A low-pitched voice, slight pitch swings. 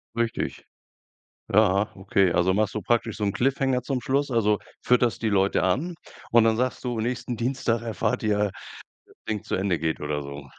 No: low, 110 Hz; average, 4.0 semitones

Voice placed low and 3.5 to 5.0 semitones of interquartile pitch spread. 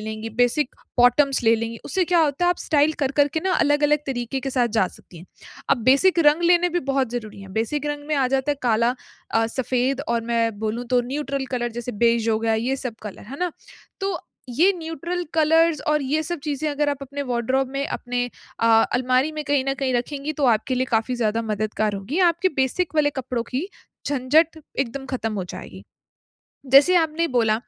No: very high, 265 Hz; average, 4.2 semitones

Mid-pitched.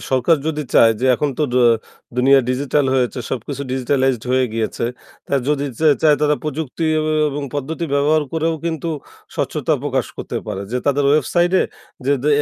Yes: medium, 145 Hz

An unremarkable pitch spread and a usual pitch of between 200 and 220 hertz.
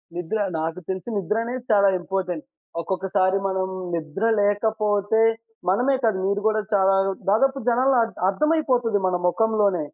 Yes: average, 3.1 semitones; high, 205 Hz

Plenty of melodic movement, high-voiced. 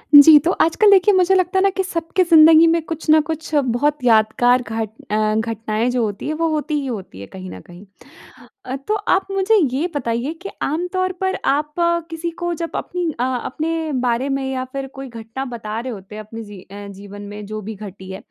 Yes: wide, 7.2 semitones; very high, 270 Hz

